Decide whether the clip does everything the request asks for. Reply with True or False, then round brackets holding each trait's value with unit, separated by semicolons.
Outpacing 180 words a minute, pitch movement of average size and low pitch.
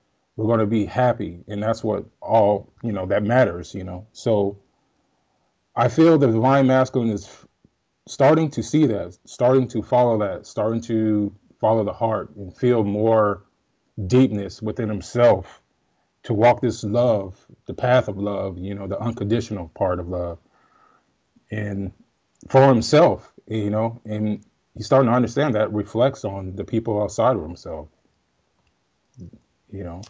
False (155 wpm; 3.4 semitones; 110 Hz)